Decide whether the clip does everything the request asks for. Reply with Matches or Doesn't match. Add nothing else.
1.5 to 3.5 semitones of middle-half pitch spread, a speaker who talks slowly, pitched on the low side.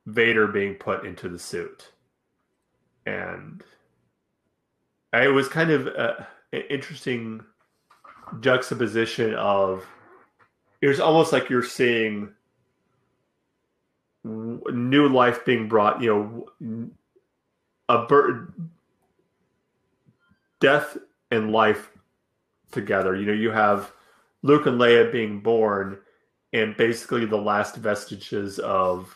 Matches